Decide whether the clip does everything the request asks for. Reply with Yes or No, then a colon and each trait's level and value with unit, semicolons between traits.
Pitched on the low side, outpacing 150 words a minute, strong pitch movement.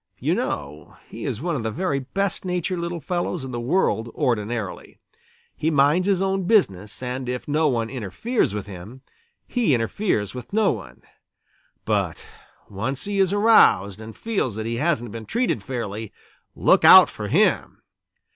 Yes: low, 130 Hz; average, 165 wpm; wide, 8.6 semitones